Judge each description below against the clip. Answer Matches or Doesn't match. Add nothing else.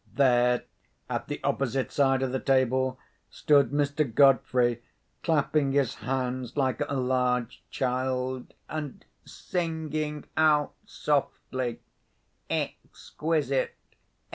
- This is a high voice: Doesn't match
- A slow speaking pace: Matches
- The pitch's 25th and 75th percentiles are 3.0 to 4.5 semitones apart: Doesn't match